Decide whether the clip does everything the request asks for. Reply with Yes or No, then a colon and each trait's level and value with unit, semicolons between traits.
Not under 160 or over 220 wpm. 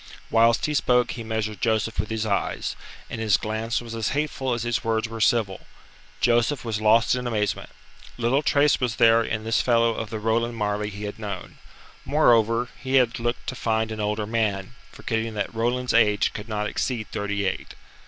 Yes: average, 190 wpm